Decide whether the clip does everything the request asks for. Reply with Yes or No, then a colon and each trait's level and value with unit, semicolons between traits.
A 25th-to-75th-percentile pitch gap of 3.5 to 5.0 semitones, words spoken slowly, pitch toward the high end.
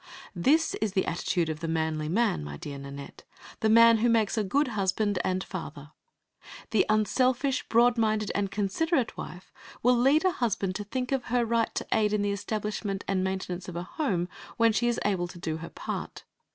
No: average, 4.6 semitones; average, 195 wpm; high, 210 Hz